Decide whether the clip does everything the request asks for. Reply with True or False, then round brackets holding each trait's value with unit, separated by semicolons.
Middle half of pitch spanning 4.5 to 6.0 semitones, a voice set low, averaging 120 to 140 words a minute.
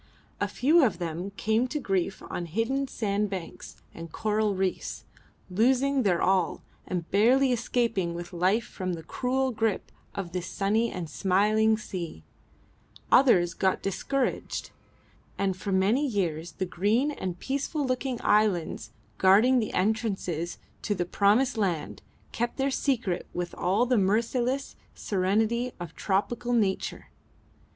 False (4.9 semitones; 205 Hz; 135 wpm)